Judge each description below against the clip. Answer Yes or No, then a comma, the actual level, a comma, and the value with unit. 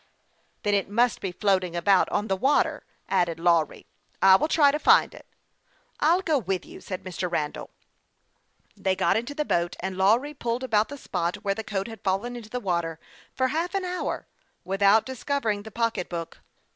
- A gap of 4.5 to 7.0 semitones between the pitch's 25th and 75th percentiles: Yes, wide, 5.4 semitones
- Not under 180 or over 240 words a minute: Yes, average, 195 wpm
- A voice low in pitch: No, high, 205 Hz